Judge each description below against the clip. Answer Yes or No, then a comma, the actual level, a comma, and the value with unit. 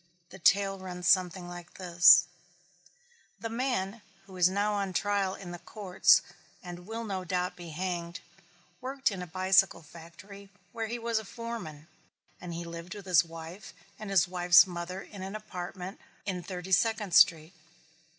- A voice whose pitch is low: No, medium, 185 Hz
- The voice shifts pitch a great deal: No, narrow, 2.5 semitones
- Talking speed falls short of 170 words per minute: Yes, average, 160 wpm